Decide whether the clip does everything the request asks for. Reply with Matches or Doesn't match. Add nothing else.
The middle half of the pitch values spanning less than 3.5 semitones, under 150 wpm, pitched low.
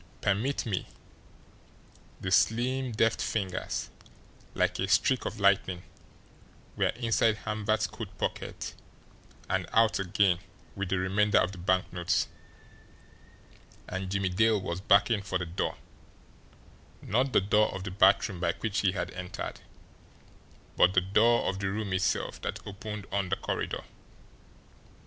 Matches